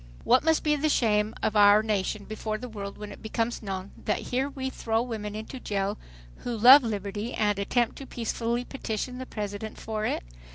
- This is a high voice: Yes, high, 220 Hz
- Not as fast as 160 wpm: No, average, 195 wpm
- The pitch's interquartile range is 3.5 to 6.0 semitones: No, average, 3.0 semitones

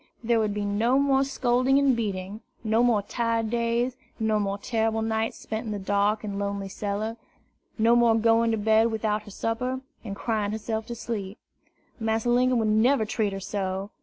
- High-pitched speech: Yes, high, 220 Hz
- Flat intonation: Yes, narrow, 2.2 semitones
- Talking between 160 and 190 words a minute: Yes, average, 185 wpm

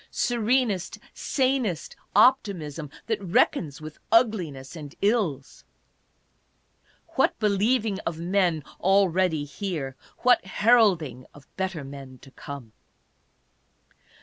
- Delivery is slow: Yes, slow, 95 wpm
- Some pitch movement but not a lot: No, wide, 6.6 semitones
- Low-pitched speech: No, medium, 180 Hz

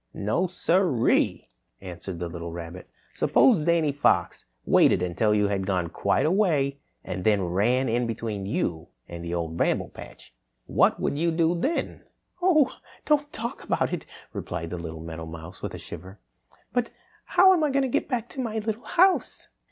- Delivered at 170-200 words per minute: Yes, average, 175 wpm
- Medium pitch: No, low, 120 Hz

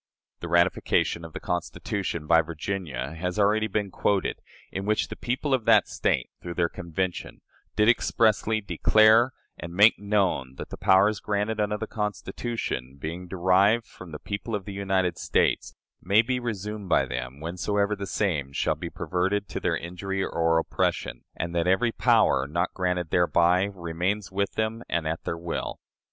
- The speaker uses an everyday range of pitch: Yes, average, 3.7 semitones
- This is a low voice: Yes, very low, 95 Hz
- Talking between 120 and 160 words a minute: No, average, 170 wpm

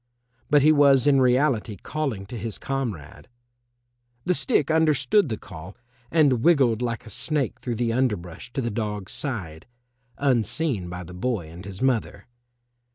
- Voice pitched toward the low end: Yes, low, 120 Hz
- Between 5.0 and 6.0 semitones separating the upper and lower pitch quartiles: Yes, wide, 5.6 semitones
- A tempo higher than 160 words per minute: No, average, 155 wpm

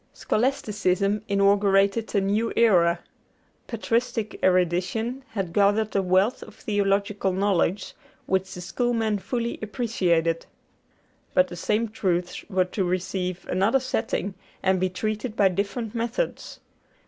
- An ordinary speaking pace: No, slow, 120 wpm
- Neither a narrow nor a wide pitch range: Yes, average, 3.1 semitones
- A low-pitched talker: No, high, 200 Hz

